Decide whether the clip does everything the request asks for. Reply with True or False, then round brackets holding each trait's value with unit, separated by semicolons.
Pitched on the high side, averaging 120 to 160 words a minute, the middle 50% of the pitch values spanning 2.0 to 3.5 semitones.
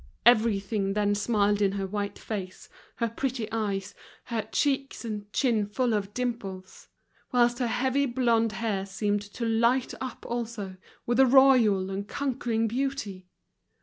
True (225 Hz; 145 wpm; 3.1 semitones)